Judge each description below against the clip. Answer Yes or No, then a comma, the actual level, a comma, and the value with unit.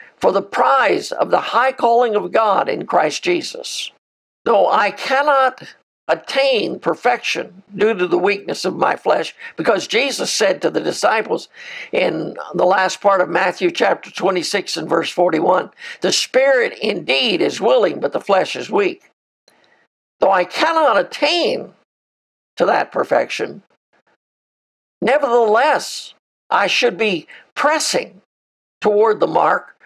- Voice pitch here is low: No, very high, 265 Hz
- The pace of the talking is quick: No, slow, 135 wpm